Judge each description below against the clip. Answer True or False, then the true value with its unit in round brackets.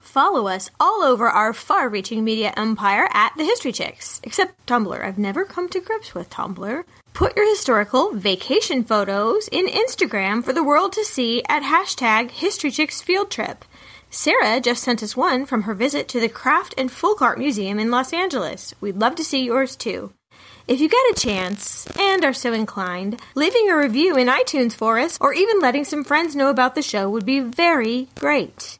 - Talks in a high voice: True (255 Hz)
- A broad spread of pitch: True (7.0 semitones)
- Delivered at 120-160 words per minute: False (190 wpm)